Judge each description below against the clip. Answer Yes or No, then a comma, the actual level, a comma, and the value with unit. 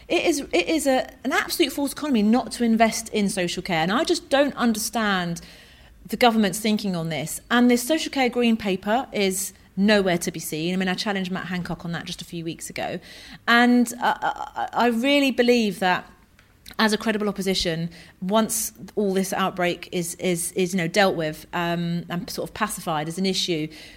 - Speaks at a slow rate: No, average, 200 wpm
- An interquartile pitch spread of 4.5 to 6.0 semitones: Yes, average, 5.2 semitones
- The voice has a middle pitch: No, high, 200 Hz